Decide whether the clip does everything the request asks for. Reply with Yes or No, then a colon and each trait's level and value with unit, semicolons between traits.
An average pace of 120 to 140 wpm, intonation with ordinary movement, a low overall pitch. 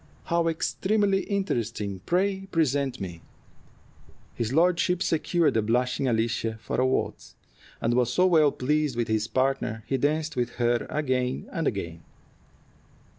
No: slow, 135 wpm; wide, 6.1 semitones; low, 130 Hz